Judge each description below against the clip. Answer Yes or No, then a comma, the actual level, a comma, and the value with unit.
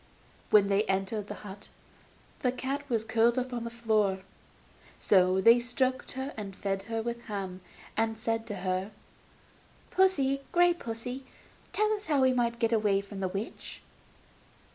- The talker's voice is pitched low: No, high, 225 Hz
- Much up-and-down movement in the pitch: No, average, 4.2 semitones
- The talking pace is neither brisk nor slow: Yes, average, 165 wpm